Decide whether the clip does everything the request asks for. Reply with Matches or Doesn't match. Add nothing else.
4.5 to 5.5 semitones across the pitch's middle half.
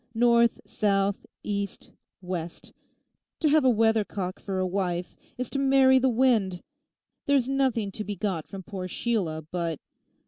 Matches